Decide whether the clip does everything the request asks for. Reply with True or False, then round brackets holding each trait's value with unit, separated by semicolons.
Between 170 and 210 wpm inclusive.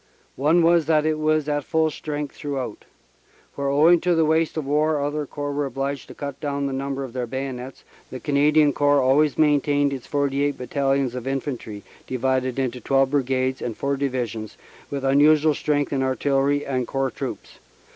True (185 wpm)